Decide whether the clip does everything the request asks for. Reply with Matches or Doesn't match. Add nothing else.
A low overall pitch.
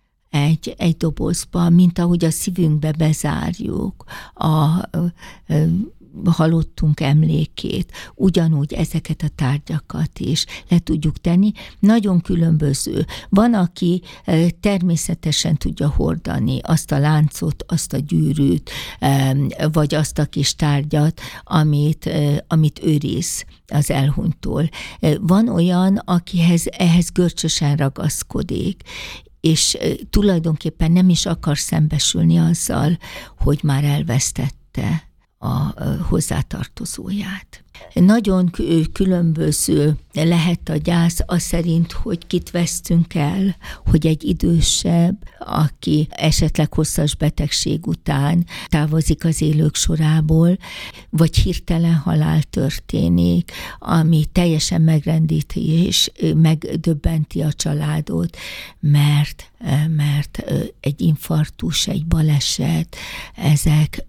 Doesn't match